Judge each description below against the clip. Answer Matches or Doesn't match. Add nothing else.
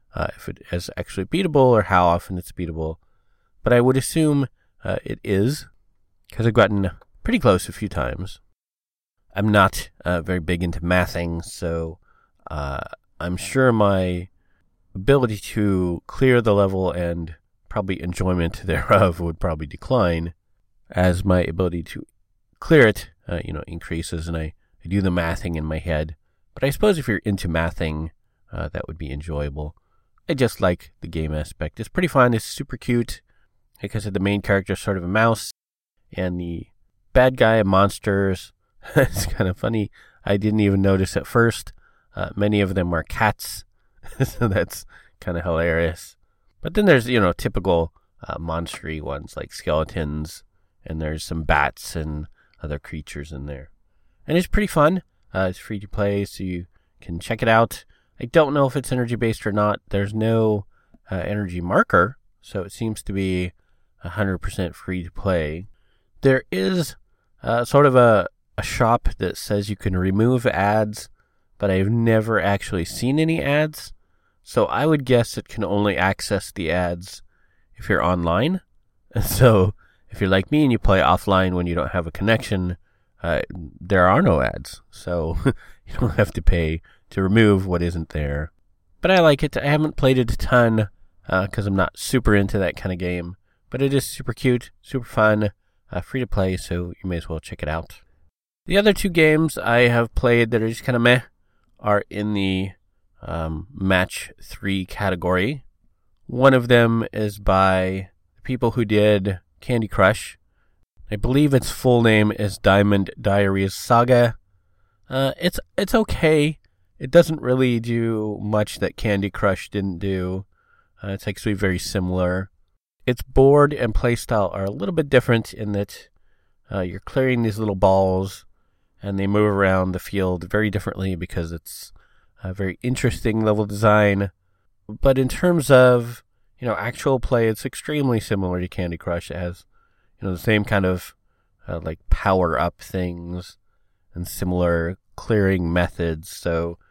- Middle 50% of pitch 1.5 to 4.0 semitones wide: Doesn't match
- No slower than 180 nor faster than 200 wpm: Doesn't match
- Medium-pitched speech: Doesn't match